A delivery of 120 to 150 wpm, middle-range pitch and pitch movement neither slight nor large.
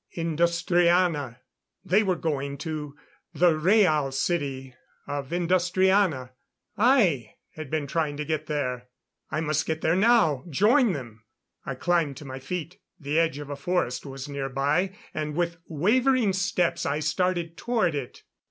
Yes: average, 145 wpm; medium, 160 Hz; average, 4.1 semitones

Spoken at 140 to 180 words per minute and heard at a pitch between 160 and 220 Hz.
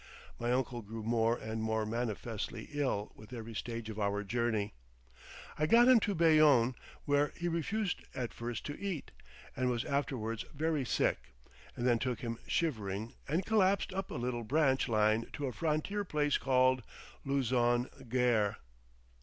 No: average, 155 wpm; low, 125 Hz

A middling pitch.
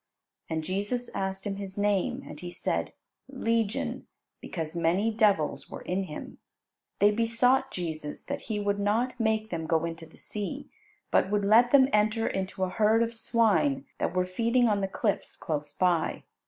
No: high, 205 Hz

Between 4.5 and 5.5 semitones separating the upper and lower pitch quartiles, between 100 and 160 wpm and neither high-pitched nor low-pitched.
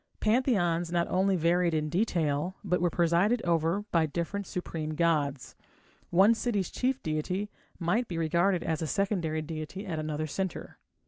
No: average, 3.7 semitones; average, 150 wpm; medium, 170 Hz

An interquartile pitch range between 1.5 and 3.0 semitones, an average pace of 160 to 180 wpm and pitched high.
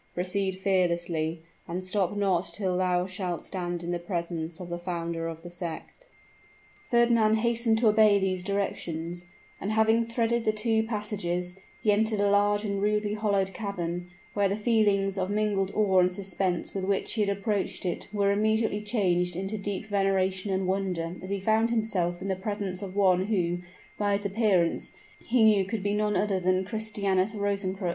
Yes: narrow, 2.6 semitones; average, 175 wpm; high, 195 Hz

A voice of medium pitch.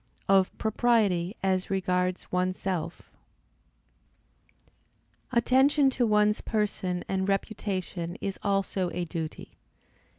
No: high, 195 Hz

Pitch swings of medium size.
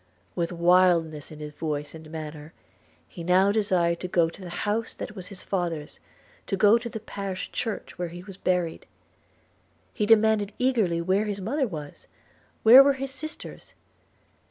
Yes: average, 4.2 semitones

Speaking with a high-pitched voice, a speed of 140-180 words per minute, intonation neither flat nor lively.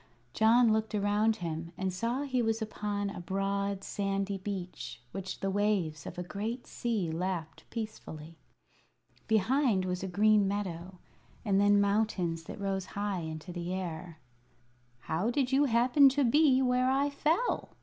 Yes: high, 200 Hz; average, 150 wpm; average, 3.9 semitones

